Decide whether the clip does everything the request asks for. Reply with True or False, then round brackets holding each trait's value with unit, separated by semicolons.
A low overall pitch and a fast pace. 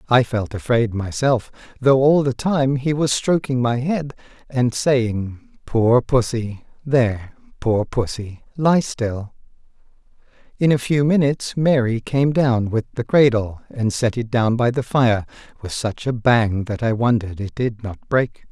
False (120 Hz; 160 wpm)